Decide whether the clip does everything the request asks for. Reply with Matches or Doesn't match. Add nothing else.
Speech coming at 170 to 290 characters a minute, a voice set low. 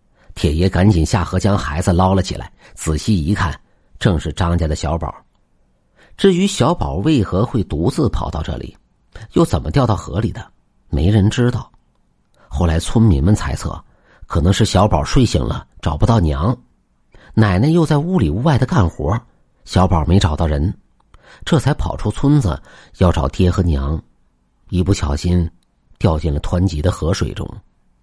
Matches